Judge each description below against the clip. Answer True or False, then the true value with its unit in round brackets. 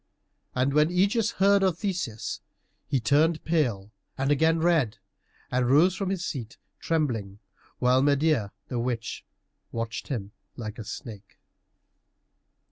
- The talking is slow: True (125 wpm)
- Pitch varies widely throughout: True (6.2 semitones)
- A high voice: False (140 Hz)